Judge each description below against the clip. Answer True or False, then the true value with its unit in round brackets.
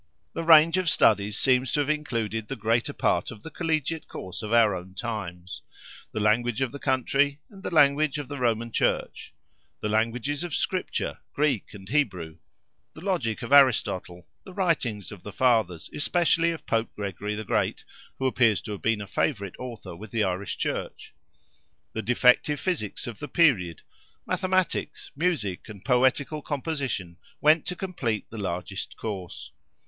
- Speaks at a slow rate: False (160 wpm)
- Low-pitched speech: True (120 Hz)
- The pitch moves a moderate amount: False (6.2 semitones)